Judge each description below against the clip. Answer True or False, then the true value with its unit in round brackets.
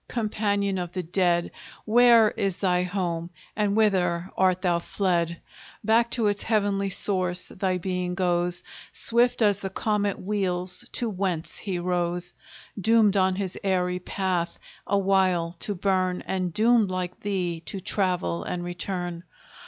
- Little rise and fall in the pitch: True (2.3 semitones)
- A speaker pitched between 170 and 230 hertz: True (185 Hz)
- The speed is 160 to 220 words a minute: False (145 wpm)